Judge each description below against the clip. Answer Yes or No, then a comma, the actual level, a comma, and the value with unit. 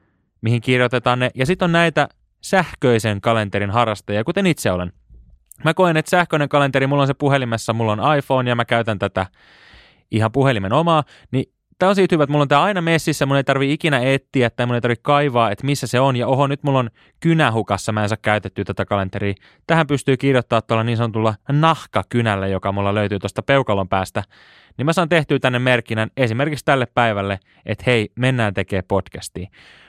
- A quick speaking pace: Yes, fast, 195 wpm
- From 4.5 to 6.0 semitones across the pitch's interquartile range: Yes, average, 5.2 semitones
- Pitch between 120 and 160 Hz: Yes, low, 125 Hz